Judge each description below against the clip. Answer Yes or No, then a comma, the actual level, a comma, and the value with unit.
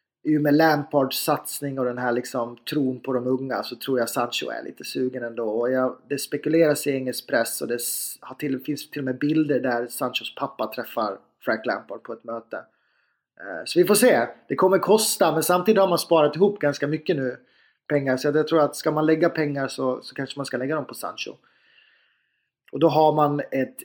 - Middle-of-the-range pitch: Yes, medium, 145 Hz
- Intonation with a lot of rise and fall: No, average, 3.4 semitones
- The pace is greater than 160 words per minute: Yes, fast, 205 wpm